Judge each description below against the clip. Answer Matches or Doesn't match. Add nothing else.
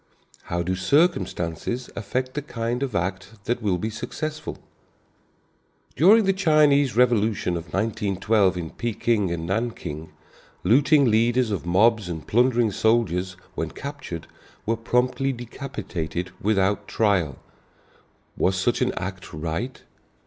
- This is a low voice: Matches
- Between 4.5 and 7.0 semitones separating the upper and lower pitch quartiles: Matches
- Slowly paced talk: Matches